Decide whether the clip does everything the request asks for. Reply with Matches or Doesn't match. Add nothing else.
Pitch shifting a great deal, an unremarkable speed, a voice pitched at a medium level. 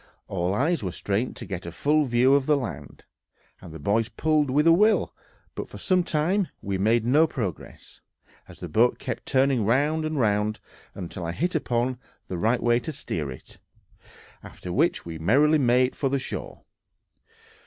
Doesn't match